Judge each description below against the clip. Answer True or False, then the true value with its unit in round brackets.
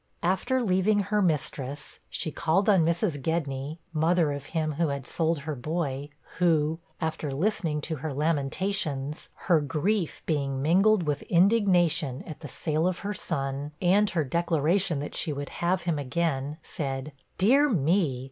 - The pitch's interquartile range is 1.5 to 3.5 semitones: False (4.1 semitones)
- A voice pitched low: False (160 Hz)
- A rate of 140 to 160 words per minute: True (155 wpm)